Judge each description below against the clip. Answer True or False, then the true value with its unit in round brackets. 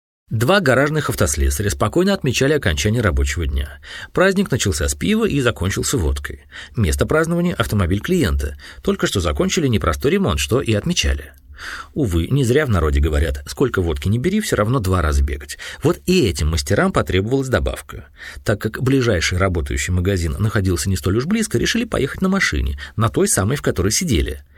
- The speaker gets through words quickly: True (165 wpm)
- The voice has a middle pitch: False (95 Hz)